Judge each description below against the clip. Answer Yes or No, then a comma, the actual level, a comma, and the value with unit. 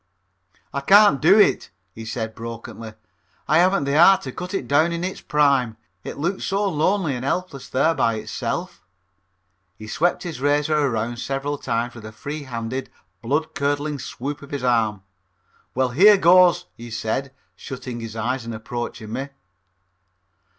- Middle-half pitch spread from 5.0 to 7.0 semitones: Yes, wide, 5.6 semitones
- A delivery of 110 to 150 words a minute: No, average, 160 wpm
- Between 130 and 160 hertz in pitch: Yes, medium, 140 Hz